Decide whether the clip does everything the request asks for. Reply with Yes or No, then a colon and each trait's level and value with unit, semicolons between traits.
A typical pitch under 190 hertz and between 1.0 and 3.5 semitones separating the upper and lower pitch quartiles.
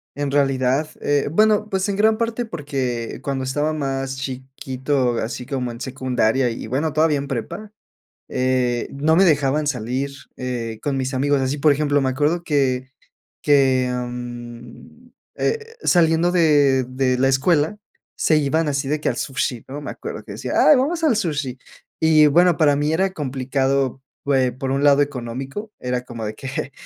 Yes: medium, 140 Hz; average, 3.1 semitones